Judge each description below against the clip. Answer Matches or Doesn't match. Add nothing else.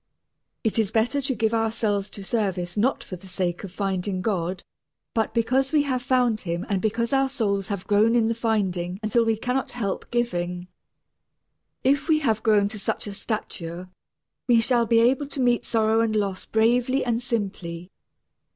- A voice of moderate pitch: Doesn't match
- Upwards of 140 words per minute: Matches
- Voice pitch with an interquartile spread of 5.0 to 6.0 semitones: Doesn't match